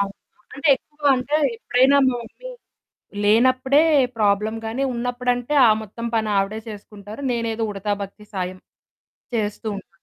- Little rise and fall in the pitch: No, average, 3.5 semitones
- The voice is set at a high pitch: Yes, high, 225 Hz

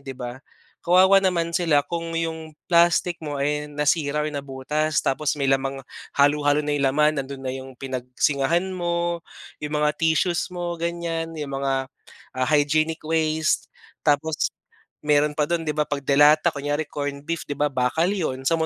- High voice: No, medium, 150 Hz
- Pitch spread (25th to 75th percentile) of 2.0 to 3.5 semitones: Yes, average, 2.8 semitones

